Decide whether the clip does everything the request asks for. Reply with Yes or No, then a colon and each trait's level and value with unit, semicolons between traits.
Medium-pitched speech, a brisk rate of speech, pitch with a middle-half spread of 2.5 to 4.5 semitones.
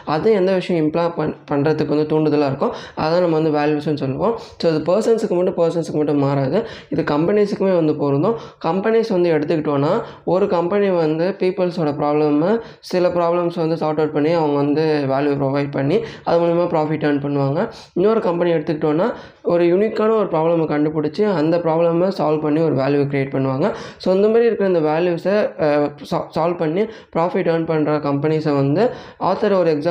Yes: medium, 160 Hz; fast, 165 wpm; average, 3.0 semitones